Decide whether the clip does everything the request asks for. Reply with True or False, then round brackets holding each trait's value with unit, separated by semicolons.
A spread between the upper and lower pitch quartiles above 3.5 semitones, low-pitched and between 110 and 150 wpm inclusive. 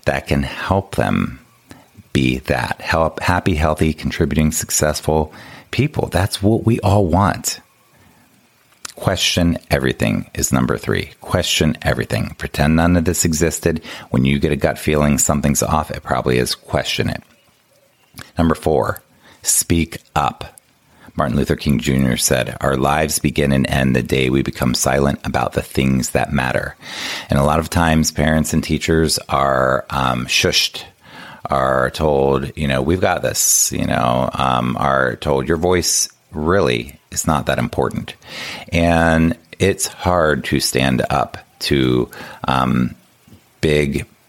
True (3.9 semitones; 75 Hz; 140 wpm)